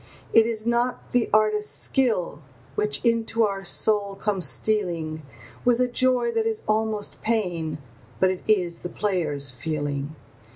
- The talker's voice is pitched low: No, high, 210 Hz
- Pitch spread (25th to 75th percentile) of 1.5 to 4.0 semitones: No, average, 4.7 semitones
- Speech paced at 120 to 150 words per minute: Yes, average, 140 wpm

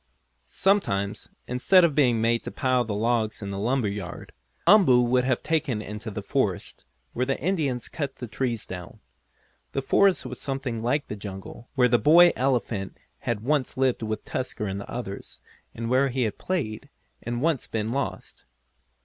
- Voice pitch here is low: Yes, low, 125 Hz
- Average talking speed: Yes, average, 175 wpm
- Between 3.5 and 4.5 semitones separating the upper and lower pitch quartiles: Yes, average, 4.0 semitones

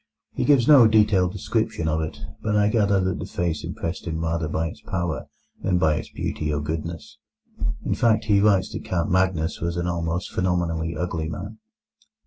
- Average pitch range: Yes, average, 3.6 semitones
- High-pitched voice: No, very low, 85 Hz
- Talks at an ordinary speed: Yes, average, 185 wpm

